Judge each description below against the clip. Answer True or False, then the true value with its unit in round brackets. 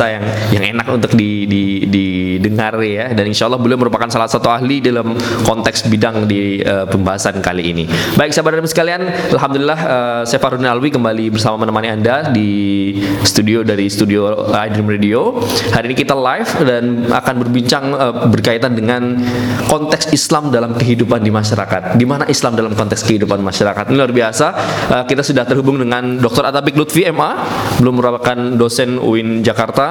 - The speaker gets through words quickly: True (165 wpm)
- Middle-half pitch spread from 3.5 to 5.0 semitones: False (3.1 semitones)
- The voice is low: True (115 Hz)